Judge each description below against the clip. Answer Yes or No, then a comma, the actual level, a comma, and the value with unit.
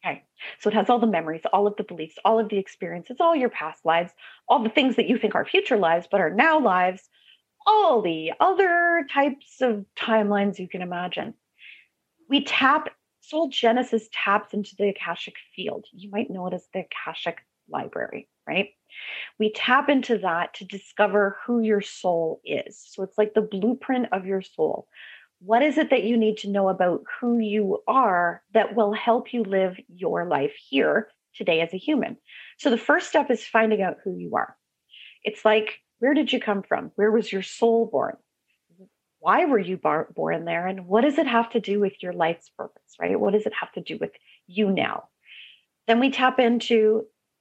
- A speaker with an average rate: Yes, average, 195 wpm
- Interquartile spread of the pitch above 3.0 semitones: Yes, average, 4.4 semitones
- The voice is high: Yes, high, 215 Hz